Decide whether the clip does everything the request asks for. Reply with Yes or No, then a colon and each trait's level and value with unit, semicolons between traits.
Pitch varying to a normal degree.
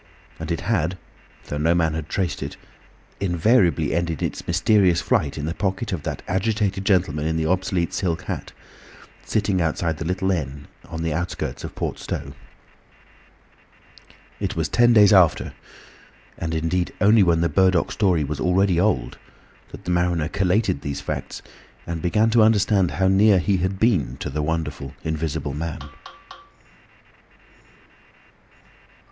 Yes: average, 3.2 semitones